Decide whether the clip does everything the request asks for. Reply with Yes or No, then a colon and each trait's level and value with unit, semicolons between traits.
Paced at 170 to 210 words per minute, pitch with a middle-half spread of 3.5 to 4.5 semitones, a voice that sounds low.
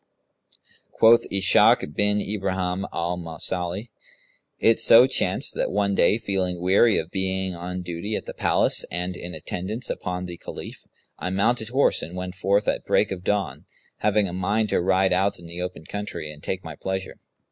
No: average, 175 wpm; narrow, 2.4 semitones; very low, 95 Hz